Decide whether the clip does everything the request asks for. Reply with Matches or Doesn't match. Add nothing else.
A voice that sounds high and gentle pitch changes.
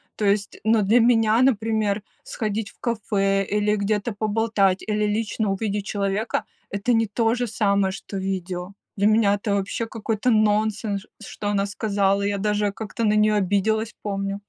Matches